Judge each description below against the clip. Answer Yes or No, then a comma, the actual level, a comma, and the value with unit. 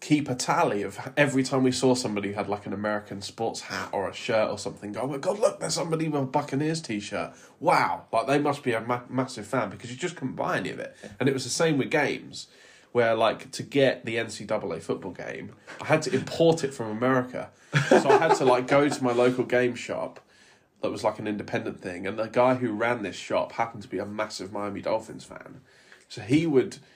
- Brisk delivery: Yes, fast, 230 wpm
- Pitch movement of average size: Yes, average, 4.2 semitones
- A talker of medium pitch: No, low, 125 Hz